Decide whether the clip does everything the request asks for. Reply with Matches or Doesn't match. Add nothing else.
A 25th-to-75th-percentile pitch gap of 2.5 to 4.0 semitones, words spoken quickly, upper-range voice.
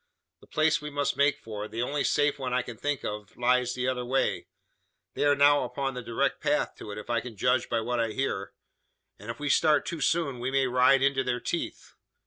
Doesn't match